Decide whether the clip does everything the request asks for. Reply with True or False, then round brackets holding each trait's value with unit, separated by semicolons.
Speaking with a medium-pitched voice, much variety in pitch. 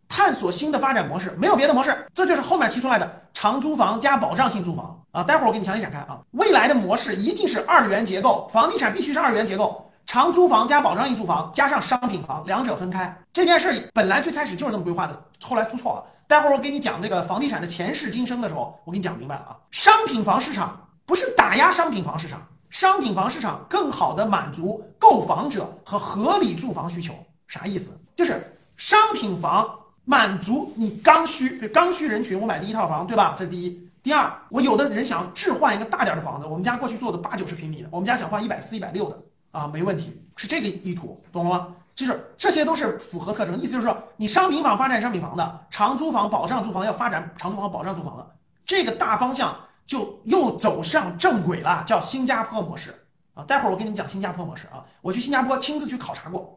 False (215 Hz; 7.6 semitones)